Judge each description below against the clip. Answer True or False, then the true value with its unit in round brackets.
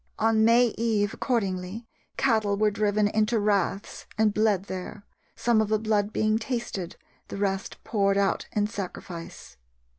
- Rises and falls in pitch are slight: True (1.8 semitones)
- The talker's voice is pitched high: True (210 Hz)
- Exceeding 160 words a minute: False (145 wpm)